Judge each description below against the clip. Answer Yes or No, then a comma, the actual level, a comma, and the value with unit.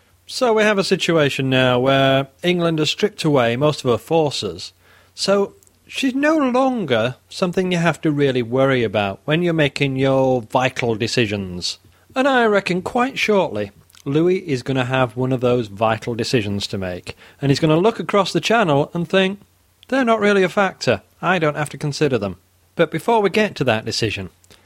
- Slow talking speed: No, average, 185 wpm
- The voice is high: No, medium, 140 Hz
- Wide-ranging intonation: Yes, wide, 8.2 semitones